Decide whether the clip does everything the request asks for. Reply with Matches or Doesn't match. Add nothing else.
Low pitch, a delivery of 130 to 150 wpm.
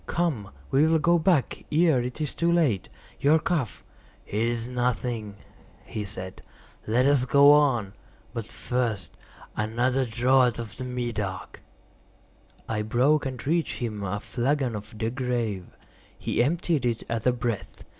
Matches